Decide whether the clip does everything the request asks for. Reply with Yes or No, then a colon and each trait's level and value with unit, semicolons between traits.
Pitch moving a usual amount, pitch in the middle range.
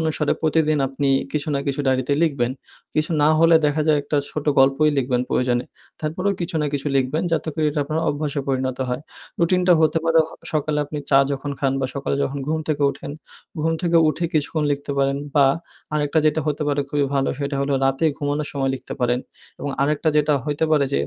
No: narrow, 2.1 semitones; medium, 145 Hz